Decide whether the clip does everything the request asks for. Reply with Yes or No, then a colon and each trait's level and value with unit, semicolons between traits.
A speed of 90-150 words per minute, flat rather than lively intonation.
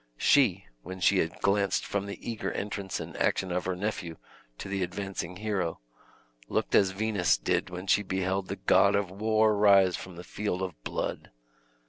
No: average, 175 wpm; narrow, 1.9 semitones